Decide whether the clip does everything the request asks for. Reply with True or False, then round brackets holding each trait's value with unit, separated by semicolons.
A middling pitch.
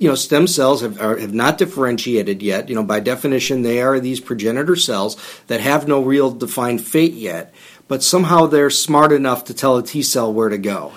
False (130 Hz)